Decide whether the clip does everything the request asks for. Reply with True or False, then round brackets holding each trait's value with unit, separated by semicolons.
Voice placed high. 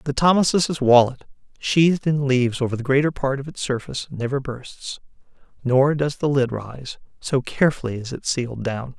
False (135 Hz)